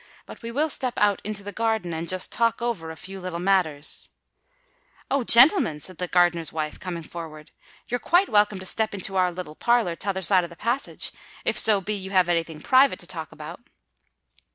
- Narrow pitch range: No, average, 4.8 semitones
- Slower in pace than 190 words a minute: No, average, 200 wpm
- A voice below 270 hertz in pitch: Yes, high, 190 Hz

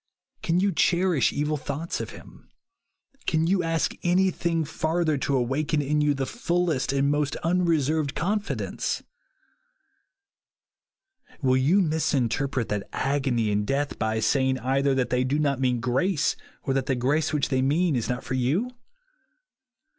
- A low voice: No, medium, 145 Hz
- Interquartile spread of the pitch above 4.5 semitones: No, average, 3.9 semitones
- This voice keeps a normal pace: Yes, average, 150 wpm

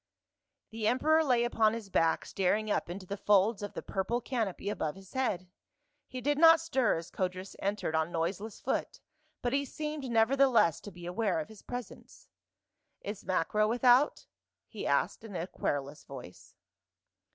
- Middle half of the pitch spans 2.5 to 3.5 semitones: No, average, 5.1 semitones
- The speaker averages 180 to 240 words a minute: No, average, 165 wpm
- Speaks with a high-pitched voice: Yes, high, 210 Hz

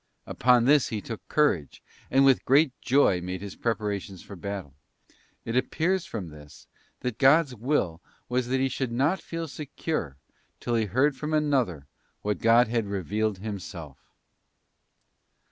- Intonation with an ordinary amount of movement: No, wide, 5.7 semitones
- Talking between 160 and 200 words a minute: No, average, 145 wpm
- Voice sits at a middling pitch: No, low, 115 Hz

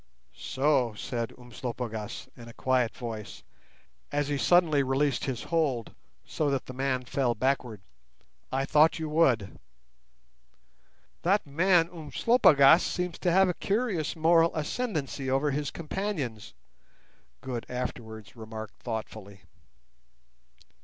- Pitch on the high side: No, low, 135 Hz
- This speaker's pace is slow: Yes, slow, 115 wpm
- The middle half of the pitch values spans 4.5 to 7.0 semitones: Yes, average, 5.3 semitones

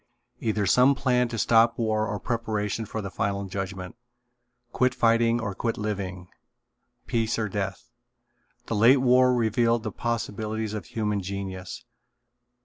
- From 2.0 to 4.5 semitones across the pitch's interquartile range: Yes, average, 2.8 semitones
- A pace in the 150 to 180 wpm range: No, average, 140 wpm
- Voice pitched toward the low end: Yes, low, 110 Hz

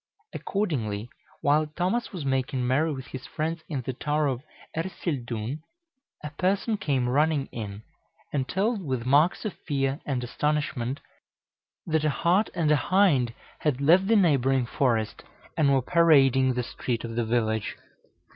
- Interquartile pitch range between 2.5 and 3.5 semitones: No, average, 4.5 semitones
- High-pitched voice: No, medium, 140 Hz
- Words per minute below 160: Yes, average, 150 wpm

